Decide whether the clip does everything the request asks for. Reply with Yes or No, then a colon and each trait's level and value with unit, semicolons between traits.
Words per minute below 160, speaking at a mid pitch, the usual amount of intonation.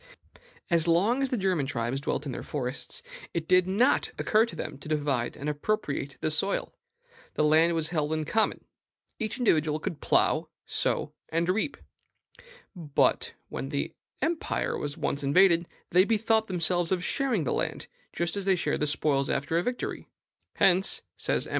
No: average, 165 wpm; medium, 170 Hz; average, 4.8 semitones